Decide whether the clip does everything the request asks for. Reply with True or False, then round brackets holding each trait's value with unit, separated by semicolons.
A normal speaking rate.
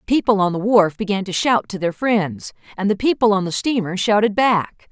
False (230 wpm)